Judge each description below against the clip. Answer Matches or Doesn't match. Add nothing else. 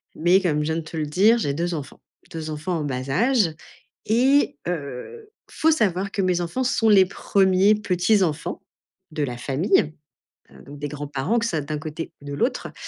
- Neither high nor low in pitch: Matches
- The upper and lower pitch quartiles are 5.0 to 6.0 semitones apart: Matches